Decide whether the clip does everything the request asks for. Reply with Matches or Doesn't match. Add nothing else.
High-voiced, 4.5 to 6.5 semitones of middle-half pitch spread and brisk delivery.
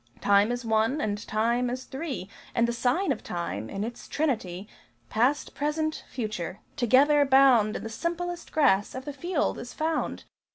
Doesn't match